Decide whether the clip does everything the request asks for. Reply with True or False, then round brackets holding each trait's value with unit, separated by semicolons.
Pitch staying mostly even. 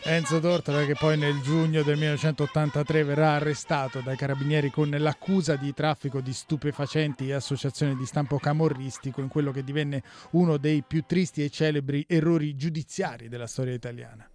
True (2.0 semitones)